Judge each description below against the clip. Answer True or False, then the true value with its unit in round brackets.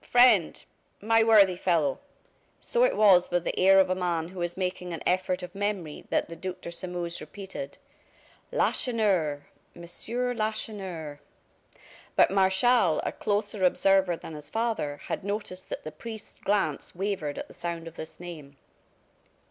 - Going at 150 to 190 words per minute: True (155 wpm)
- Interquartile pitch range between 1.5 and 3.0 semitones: False (3.4 semitones)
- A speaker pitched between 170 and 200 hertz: True (185 Hz)